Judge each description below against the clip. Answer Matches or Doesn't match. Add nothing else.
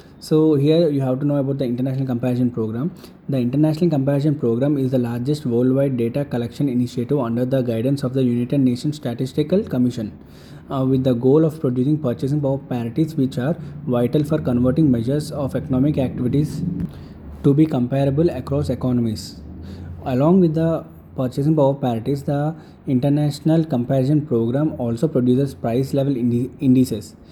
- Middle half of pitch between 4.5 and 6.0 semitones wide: Doesn't match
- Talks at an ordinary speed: Matches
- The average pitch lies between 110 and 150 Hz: Matches